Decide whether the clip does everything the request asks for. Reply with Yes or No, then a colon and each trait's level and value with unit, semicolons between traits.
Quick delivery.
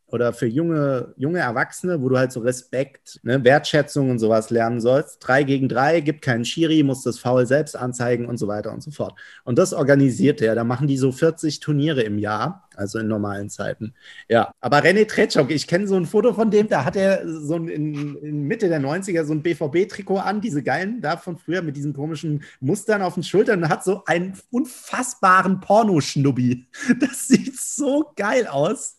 Yes: fast, 200 wpm